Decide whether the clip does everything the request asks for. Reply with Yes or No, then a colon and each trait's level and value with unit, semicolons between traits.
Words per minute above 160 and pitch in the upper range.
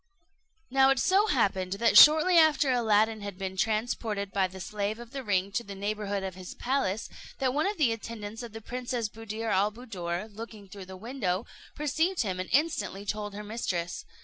Yes: average, 190 wpm; high, 215 Hz